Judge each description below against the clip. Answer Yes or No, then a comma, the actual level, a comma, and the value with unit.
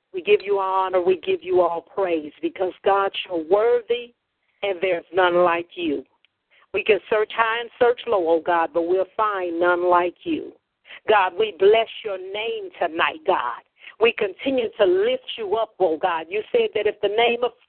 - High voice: Yes, high, 215 Hz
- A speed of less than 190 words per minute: No, average, 195 wpm